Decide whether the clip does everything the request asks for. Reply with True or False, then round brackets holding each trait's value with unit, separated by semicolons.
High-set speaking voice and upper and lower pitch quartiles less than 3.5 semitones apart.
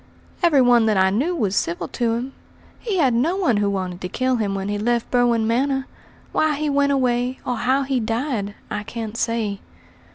False (240 Hz; 4.3 semitones)